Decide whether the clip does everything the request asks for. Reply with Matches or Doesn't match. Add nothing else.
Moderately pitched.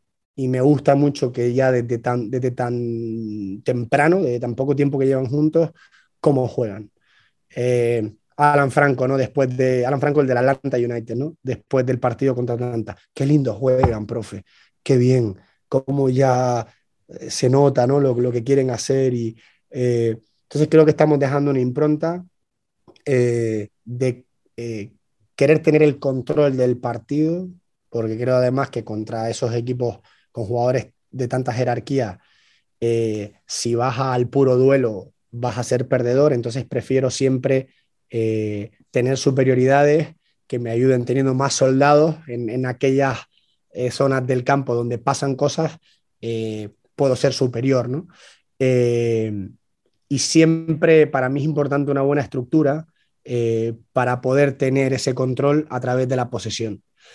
Doesn't match